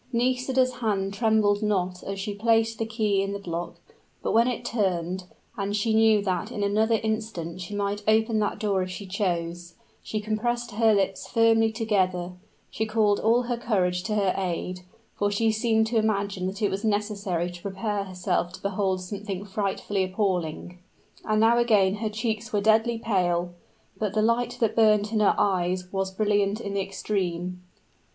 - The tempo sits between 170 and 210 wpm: Yes, average, 175 wpm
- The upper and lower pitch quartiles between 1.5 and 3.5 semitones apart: Yes, average, 2.8 semitones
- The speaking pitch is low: No, high, 205 Hz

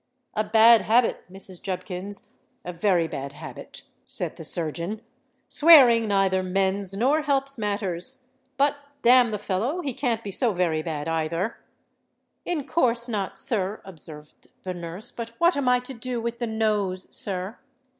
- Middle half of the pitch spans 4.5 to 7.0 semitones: Yes, average, 4.9 semitones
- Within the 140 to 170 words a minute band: Yes, average, 145 wpm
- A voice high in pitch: Yes, high, 210 Hz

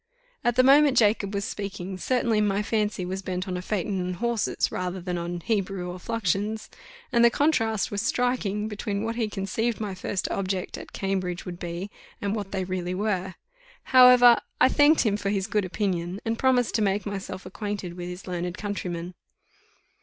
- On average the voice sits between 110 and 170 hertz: No, high, 200 Hz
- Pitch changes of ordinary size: Yes, average, 3.4 semitones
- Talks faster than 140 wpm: Yes, average, 185 wpm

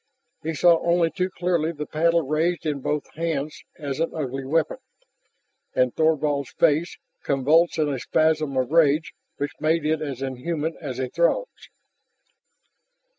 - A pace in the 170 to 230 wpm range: No, average, 145 wpm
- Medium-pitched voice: Yes, medium, 155 Hz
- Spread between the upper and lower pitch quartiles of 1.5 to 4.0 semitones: Yes, average, 2.8 semitones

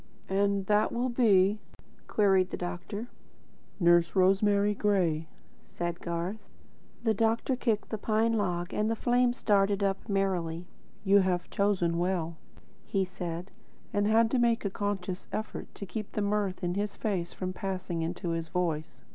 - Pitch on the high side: Yes, high, 195 Hz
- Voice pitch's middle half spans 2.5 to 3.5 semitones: Yes, average, 3.1 semitones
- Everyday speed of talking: Yes, average, 155 wpm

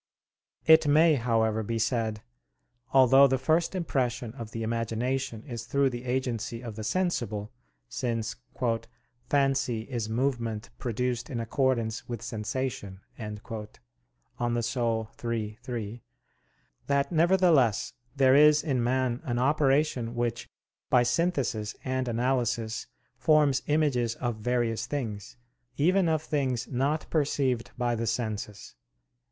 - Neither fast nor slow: No, slow, 120 wpm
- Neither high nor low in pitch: No, low, 125 Hz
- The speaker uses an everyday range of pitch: Yes, average, 3.2 semitones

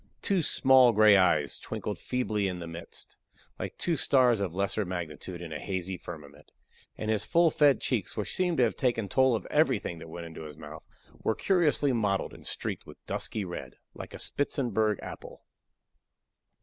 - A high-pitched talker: No, low, 105 Hz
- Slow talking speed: No, average, 175 wpm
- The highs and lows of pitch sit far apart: Yes, wide, 6.8 semitones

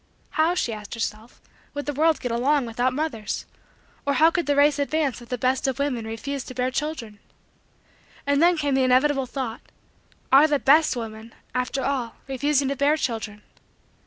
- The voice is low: No, very high, 270 Hz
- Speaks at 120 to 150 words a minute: No, average, 180 wpm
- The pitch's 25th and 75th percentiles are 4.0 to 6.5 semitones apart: No, average, 3.4 semitones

